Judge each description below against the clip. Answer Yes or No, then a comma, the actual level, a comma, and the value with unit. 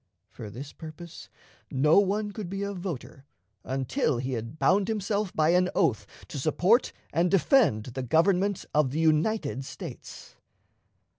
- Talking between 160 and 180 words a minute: No, average, 145 wpm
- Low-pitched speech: No, medium, 165 Hz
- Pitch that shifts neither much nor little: No, wide, 6.9 semitones